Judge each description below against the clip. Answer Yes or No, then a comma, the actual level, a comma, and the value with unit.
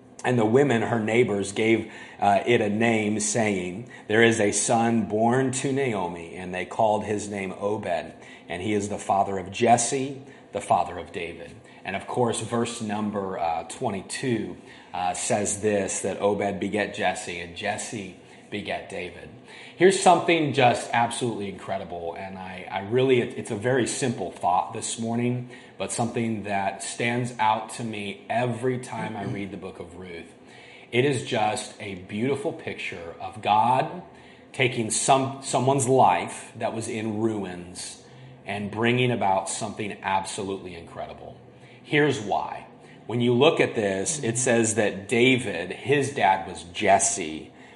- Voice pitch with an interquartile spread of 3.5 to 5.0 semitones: Yes, average, 3.8 semitones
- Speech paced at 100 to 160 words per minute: Yes, average, 150 wpm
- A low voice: Yes, low, 110 Hz